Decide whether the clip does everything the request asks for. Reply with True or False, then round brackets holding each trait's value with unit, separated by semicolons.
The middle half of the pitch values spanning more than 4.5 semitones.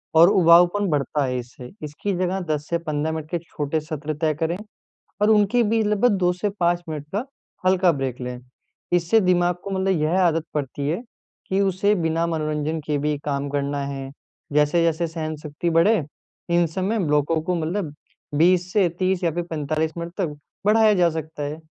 False (3.5 semitones)